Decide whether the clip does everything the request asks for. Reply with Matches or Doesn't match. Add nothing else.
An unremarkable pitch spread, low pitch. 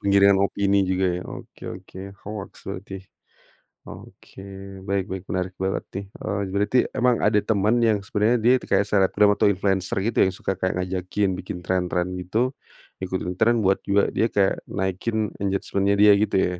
Doesn't match